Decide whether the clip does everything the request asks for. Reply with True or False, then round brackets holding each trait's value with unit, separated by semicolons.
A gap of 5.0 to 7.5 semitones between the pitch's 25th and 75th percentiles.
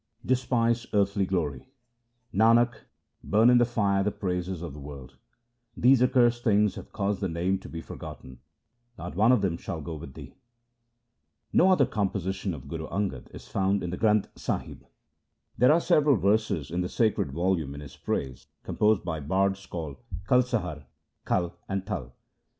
True (5.4 semitones)